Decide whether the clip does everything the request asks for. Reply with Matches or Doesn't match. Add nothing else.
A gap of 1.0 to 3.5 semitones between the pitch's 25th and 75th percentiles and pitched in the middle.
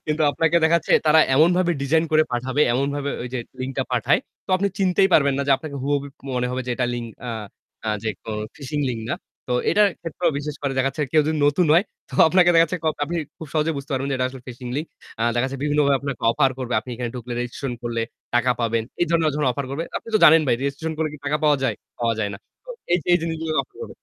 Doesn't match